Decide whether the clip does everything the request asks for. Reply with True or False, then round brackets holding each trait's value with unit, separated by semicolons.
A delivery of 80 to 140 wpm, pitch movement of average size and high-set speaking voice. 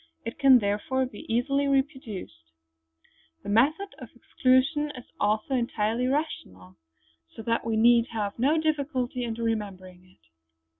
True (135 wpm; 4.3 semitones; 235 Hz)